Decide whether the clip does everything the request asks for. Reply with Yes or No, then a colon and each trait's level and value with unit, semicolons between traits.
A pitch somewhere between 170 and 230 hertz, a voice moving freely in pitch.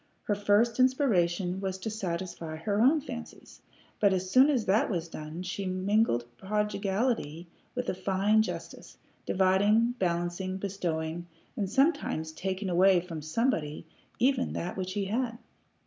No: high, 190 Hz; average, 3.9 semitones